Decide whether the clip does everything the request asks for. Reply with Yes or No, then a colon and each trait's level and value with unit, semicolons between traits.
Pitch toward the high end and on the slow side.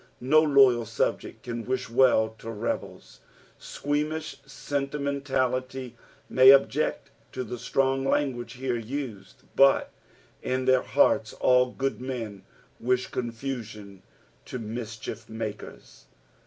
No: low, 130 Hz; slow, 105 wpm